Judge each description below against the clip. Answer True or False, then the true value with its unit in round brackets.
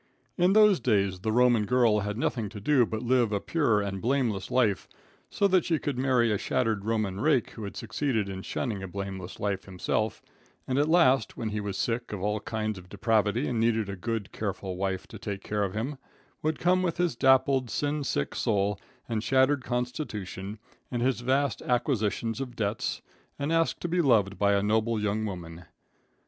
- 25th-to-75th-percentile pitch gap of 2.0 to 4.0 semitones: False (4.4 semitones)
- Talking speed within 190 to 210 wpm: True (195 wpm)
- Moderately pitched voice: False (110 Hz)